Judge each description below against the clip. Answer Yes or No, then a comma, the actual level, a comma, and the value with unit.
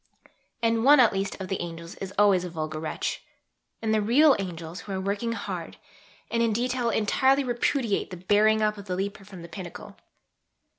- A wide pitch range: No, average, 4.1 semitones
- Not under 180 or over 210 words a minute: Yes, average, 190 wpm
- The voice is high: Yes, high, 205 Hz